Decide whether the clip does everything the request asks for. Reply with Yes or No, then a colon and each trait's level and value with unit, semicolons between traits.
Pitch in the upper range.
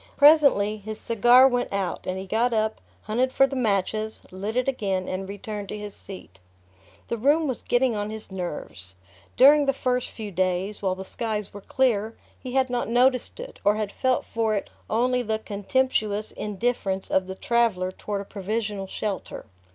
Yes: high, 215 Hz